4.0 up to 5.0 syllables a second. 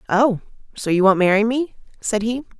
No: 5.3 syllables/s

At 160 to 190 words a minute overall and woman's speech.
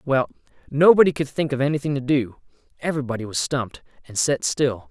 No: average, 170 wpm; male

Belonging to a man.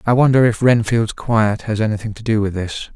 Yes: male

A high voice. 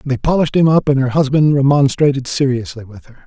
No: low, 135 Hz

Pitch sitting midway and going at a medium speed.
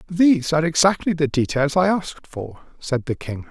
Yes: medium, 155 Hz; average, 190 wpm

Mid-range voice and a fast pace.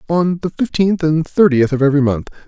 No: medium, 155 Hz; average, 195 wpm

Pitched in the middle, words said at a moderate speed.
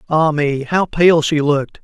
Yes: medium, 155 Hz; average, 195 wpm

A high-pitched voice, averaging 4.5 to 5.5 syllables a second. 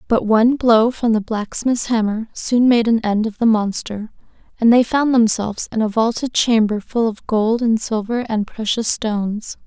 Yes: high, 225 Hz; 4.6 syllables/s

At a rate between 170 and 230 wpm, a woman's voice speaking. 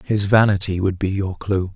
No: fast, 205 wpm; male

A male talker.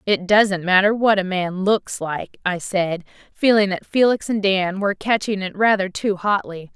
No: female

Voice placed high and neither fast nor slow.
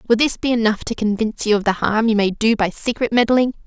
No: high, 225 Hz; fast, 260 wpm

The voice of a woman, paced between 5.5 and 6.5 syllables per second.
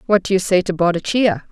Yes: female; 5.9 syllables/s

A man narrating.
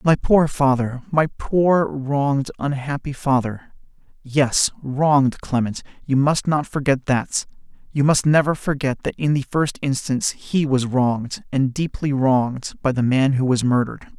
Yes: male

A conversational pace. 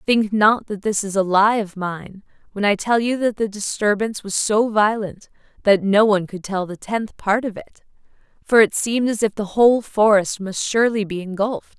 No: fast, 210 wpm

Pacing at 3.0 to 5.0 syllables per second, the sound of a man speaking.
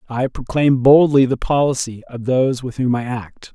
Yes: 4.9 syllables/s; male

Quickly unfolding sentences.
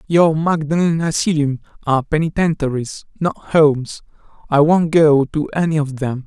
No: slow, 135 wpm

